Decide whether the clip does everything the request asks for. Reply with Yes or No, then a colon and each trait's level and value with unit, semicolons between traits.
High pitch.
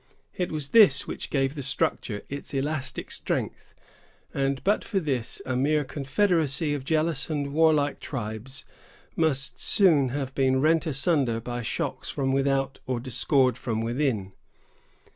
No: low, 135 Hz